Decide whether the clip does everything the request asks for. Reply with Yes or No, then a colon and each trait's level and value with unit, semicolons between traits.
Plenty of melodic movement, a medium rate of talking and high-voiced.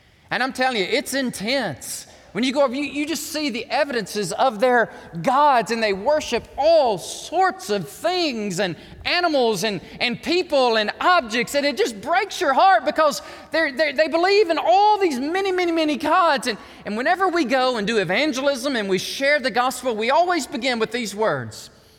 Yes: wide, 6.0 semitones; average, 190 wpm; very high, 275 Hz